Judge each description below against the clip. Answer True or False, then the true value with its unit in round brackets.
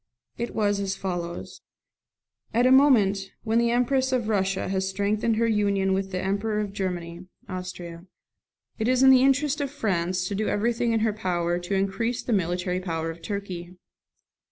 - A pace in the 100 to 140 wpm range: False (175 wpm)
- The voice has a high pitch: True (200 Hz)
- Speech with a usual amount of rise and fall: True (4.1 semitones)